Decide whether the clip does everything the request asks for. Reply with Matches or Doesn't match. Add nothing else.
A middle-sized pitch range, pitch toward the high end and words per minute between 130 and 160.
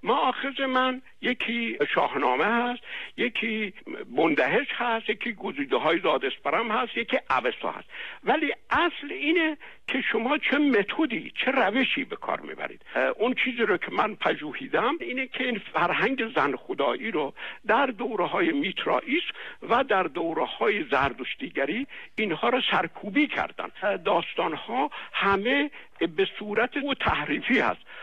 Matches